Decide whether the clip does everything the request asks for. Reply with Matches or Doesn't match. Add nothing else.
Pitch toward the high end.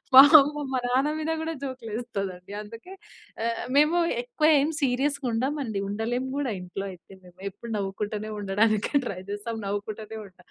Matches